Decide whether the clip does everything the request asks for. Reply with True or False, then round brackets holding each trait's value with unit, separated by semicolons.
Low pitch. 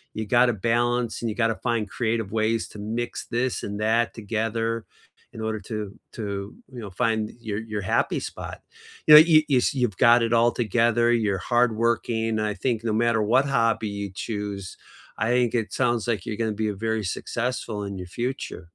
True (115 Hz)